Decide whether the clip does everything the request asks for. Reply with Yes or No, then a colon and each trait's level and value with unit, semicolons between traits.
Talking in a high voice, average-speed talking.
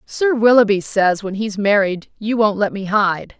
Yes: high, 210 Hz; average, 195 wpm